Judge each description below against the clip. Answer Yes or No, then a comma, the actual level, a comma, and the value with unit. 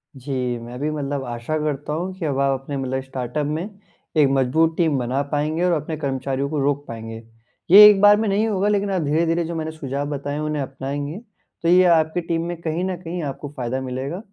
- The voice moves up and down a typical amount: Yes, average, 3.7 semitones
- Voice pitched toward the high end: No, medium, 150 Hz